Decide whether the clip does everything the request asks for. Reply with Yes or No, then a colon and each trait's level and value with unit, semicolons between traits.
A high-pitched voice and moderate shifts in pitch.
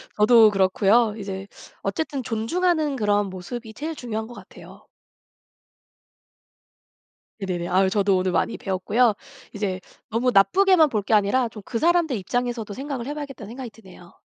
Yes: high, 220 Hz; average, 4.6 semitones